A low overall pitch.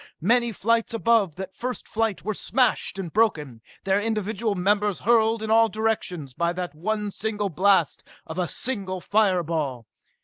No: high, 205 Hz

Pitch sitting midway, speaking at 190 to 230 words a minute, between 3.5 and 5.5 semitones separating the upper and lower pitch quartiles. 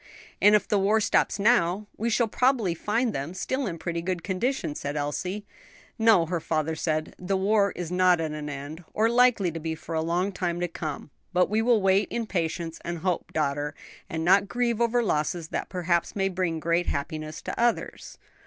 Yes: medium, 180 Hz; average, 200 wpm; average, 4.5 semitones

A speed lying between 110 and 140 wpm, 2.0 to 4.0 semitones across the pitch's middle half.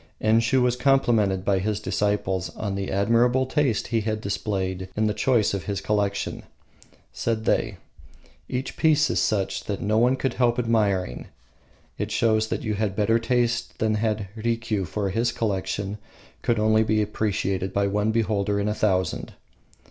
No: average, 165 wpm; narrow, 2.5 semitones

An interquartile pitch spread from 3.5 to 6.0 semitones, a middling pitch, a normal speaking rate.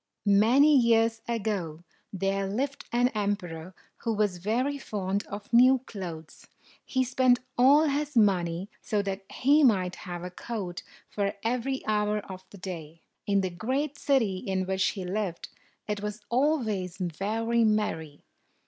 No: average, 4.4 semitones; high, 210 Hz; average, 145 wpm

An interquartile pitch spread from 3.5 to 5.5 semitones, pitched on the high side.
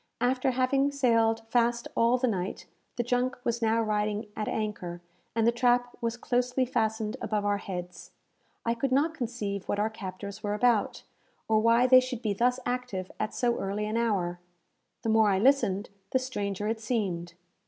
No: average, 3.1 semitones; high, 225 Hz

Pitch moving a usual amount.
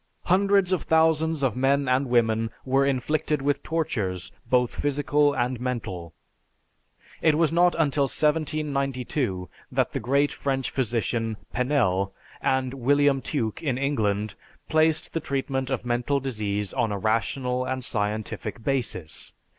Yes: average, 4.1 semitones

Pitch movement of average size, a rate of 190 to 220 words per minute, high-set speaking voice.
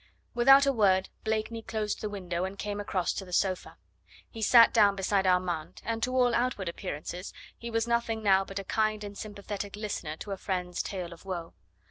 Yes: average, 3.2 semitones; average, 195 wpm; high, 205 Hz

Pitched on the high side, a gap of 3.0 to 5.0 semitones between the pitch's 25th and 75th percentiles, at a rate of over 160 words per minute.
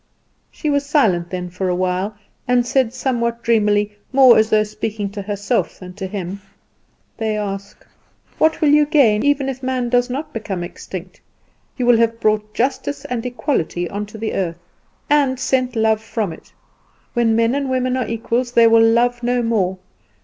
Yes: high, 225 Hz; average, 3.6 semitones; average, 180 wpm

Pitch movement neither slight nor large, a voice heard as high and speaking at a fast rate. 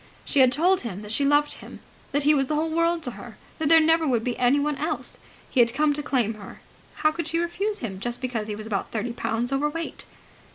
Yes: average, 4.9 semitones; very high, 280 Hz; fast, 240 wpm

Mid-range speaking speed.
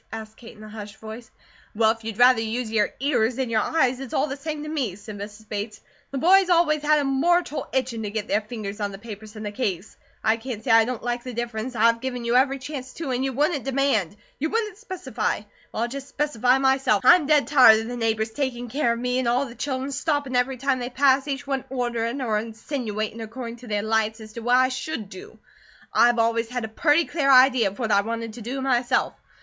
No: fast, 240 wpm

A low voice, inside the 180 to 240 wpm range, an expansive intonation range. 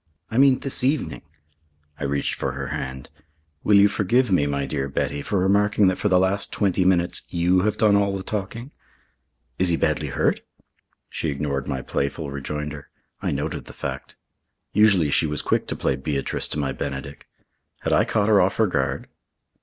Yes: very low, 90 Hz; average, 185 wpm; wide, 6.2 semitones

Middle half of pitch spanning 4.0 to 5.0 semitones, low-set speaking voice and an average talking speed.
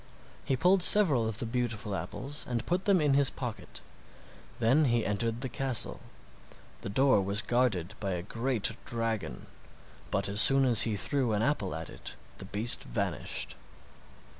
Yes: average, 4.6 semitones; low, 115 Hz; average, 165 wpm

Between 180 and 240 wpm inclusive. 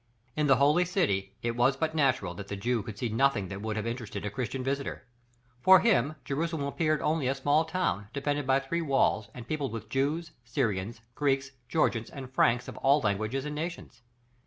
Yes: average, 195 wpm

